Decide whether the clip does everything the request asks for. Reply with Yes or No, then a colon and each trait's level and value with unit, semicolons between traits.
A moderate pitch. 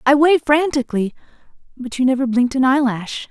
No: very high, 265 Hz